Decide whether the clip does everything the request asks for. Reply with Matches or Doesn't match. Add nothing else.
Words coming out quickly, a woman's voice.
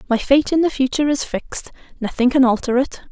Doesn't match